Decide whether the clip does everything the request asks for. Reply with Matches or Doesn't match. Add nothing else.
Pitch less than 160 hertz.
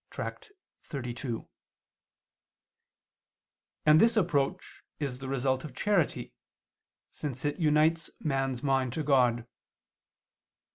Matches